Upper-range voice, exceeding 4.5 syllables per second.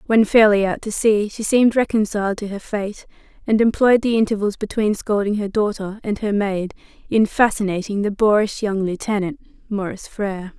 Yes: high, 210 Hz; 5.4 syllables/s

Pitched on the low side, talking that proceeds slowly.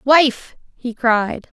No: high, 245 Hz; slow, 115 wpm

